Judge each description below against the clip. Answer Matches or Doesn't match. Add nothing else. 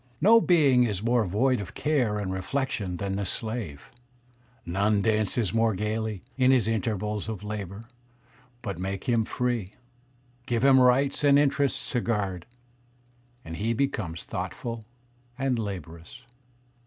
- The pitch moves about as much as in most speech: Matches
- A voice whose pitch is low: Matches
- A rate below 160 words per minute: Matches